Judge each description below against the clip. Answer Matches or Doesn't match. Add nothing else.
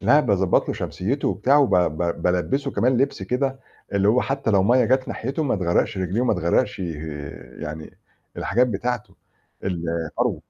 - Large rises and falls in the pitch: Matches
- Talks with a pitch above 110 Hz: Doesn't match